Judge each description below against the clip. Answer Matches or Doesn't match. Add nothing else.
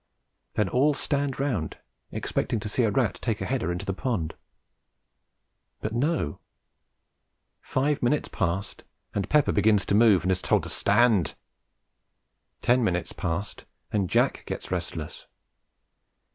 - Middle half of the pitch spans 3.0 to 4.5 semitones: Doesn't match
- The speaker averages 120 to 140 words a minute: Matches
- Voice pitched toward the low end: Matches